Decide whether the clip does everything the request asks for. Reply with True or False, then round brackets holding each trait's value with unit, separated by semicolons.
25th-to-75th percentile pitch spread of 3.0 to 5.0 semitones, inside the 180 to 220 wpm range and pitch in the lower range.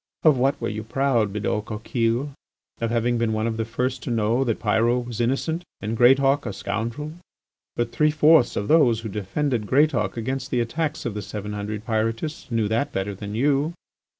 True (3.8 semitones; 190 wpm; 115 Hz)